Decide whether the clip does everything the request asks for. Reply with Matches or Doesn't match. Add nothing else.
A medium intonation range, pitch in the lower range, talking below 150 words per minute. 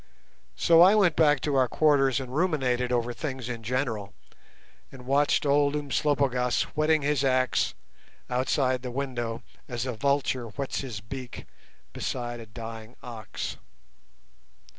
Matches